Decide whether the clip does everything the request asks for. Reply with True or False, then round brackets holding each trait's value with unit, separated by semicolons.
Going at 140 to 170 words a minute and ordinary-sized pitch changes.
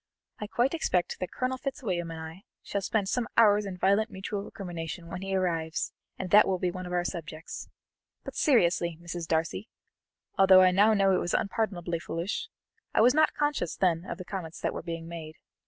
False (195 wpm; 3.4 semitones)